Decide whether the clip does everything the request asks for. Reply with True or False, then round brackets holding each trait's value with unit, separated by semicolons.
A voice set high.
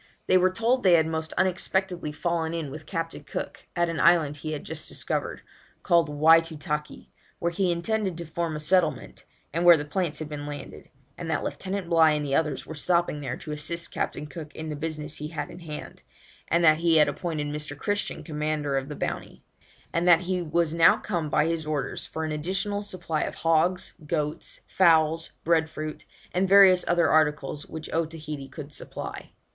False (160 Hz)